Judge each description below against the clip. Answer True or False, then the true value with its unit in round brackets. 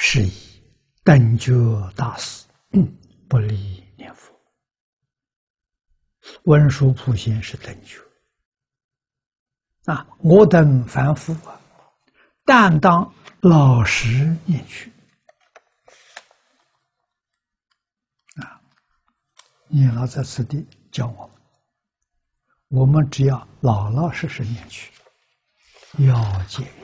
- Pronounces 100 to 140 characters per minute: True (110 characters per minute)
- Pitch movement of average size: True (4.4 semitones)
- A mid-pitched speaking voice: False (130 Hz)